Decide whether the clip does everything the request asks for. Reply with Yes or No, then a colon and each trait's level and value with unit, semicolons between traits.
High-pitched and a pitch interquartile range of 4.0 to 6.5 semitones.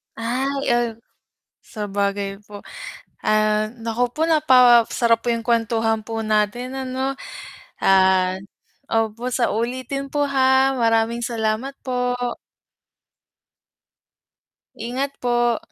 No: high, 235 Hz; average, 3.0 semitones